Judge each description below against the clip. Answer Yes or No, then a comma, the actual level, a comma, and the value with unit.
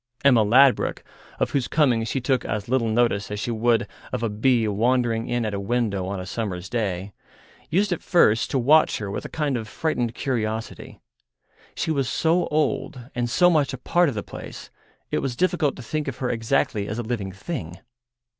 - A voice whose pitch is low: Yes, low, 120 Hz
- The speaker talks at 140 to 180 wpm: No, average, 200 wpm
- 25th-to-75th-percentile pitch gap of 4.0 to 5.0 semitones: Yes, average, 4.3 semitones